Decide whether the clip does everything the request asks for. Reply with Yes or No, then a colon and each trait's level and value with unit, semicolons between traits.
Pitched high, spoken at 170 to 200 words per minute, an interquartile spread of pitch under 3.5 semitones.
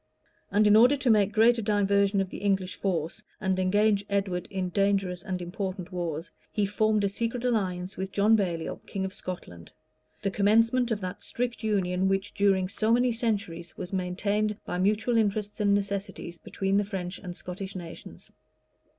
Yes: high, 200 Hz; average, 175 wpm; narrow, 2.5 semitones